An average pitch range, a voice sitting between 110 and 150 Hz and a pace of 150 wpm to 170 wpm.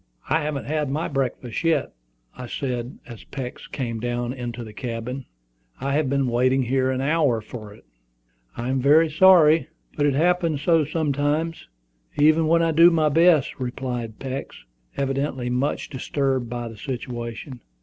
Yes: average, 3.8 semitones; low, 135 Hz; average, 160 wpm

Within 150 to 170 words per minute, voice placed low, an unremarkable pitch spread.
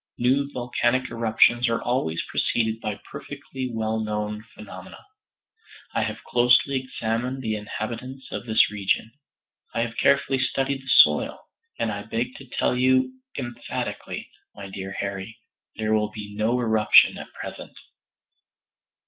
No: slow, 135 wpm; low, 115 Hz; average, 3.1 semitones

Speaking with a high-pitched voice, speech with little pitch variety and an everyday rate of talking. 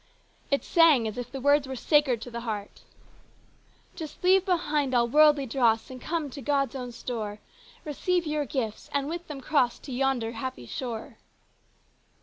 No: very high, 270 Hz; average, 4.0 semitones; average, 165 wpm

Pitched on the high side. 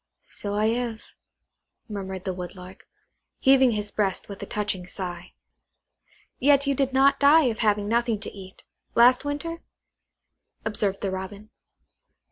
Yes: high, 215 Hz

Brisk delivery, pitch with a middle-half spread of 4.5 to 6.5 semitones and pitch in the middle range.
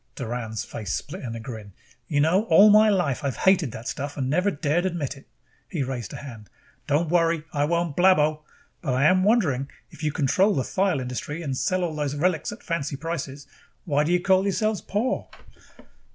No: average, 195 wpm; average, 5.1 semitones; medium, 150 Hz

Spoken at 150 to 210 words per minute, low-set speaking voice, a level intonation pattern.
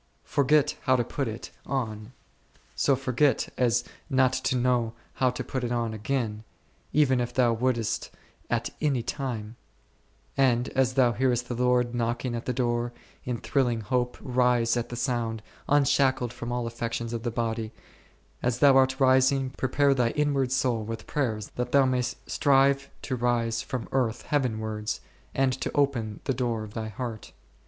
Yes: average, 165 wpm; low, 125 Hz; narrow, 2.3 semitones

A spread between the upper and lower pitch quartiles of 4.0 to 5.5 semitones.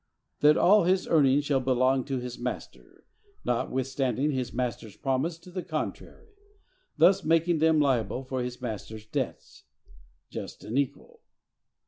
Yes: average, 4.4 semitones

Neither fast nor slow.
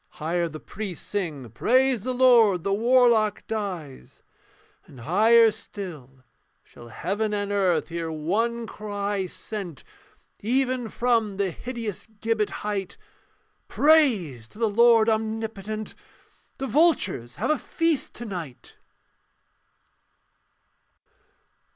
No: slow, 110 wpm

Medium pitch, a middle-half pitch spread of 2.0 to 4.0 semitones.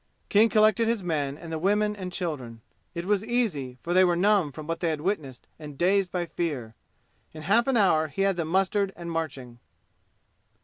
No: medium, 175 Hz; average, 4.5 semitones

